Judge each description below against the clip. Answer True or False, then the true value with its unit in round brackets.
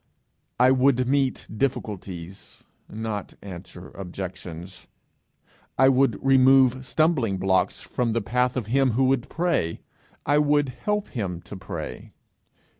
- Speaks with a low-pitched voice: True (125 Hz)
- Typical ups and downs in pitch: False (5.7 semitones)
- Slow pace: True (120 wpm)